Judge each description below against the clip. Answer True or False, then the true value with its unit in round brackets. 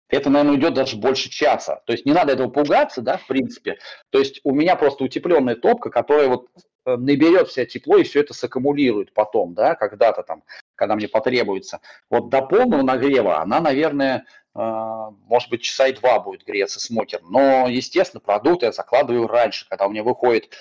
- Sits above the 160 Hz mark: False (130 Hz)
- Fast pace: True (180 wpm)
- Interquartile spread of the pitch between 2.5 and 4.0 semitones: True (3.3 semitones)